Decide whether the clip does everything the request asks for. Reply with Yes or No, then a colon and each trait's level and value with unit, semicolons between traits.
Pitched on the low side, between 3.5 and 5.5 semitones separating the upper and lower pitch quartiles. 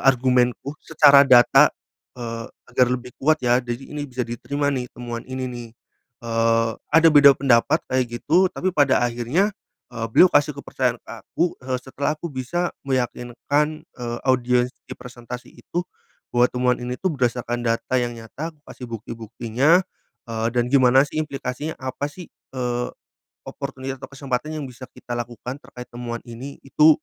No: low, 125 Hz; average, 2.8 semitones